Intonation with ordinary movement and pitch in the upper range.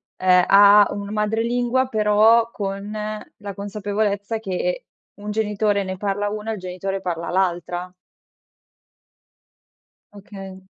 No: narrow, 1.8 semitones; high, 205 Hz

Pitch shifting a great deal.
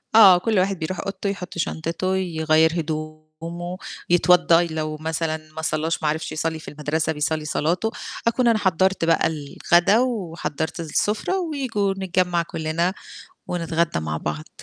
No: average, 3.1 semitones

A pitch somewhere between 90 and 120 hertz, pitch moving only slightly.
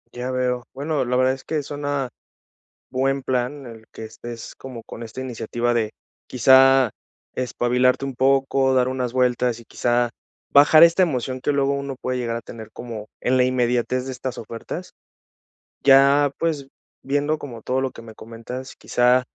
No: low, 130 Hz; narrow, 2.1 semitones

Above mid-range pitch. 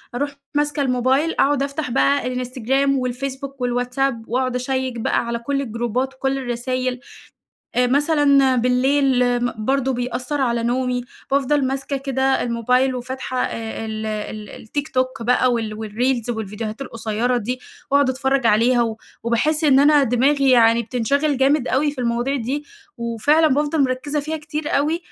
Yes: very high, 255 Hz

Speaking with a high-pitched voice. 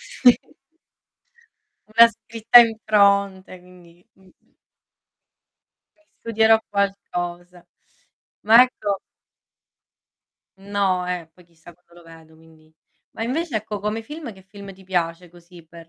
Yes: high, 195 Hz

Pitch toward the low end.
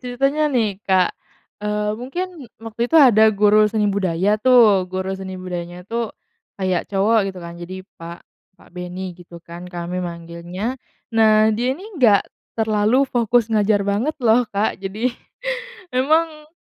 No: high, 210 Hz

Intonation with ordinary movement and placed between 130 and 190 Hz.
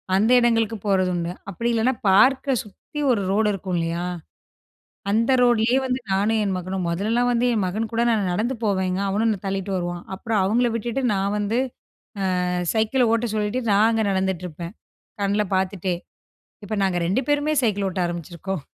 No: average, 3.4 semitones; high, 205 Hz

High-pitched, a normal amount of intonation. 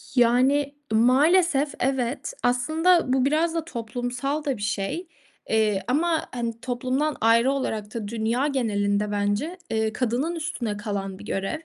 Yes: high, 245 Hz; average, 4.9 semitones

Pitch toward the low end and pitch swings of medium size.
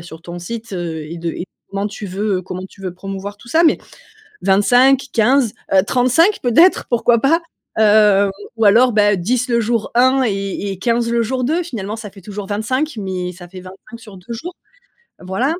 No: high, 210 Hz; average, 4.2 semitones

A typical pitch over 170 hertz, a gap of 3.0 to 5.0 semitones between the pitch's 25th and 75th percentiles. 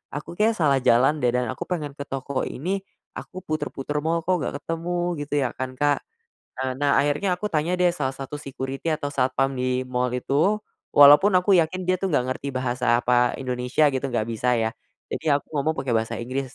No: medium, 140 Hz; average, 4.1 semitones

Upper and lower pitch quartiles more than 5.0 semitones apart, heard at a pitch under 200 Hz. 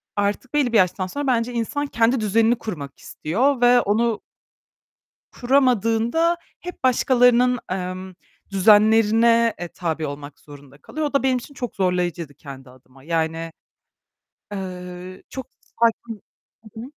No: wide, 5.6 semitones; high, 220 Hz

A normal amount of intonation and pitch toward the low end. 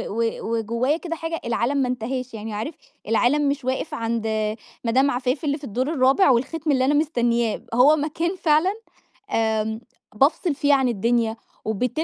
No: average, 4.3 semitones; very high, 255 Hz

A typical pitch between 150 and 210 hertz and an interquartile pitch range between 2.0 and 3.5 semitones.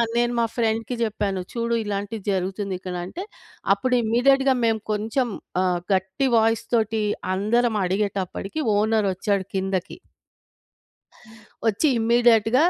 No: high, 220 Hz; average, 3.2 semitones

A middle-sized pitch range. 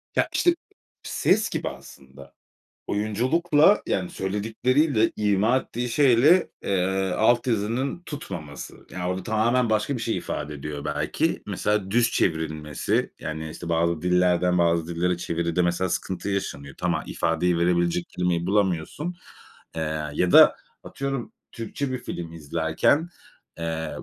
No: wide, 5.8 semitones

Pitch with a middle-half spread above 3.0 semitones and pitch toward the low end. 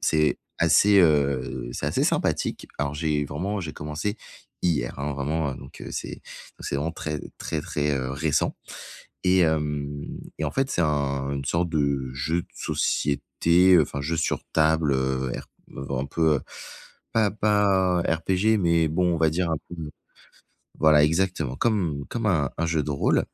Yes: average, 3.6 semitones; very low, 80 Hz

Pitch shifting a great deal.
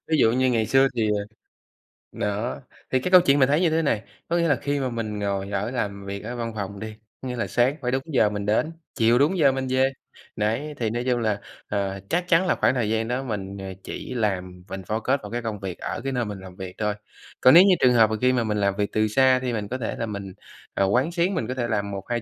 No: average, 4.2 semitones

